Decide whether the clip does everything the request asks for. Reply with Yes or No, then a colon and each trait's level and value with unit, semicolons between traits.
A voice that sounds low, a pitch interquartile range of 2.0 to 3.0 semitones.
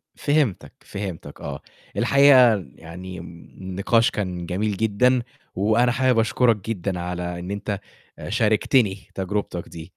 No: low, 100 Hz; average, 4.2 semitones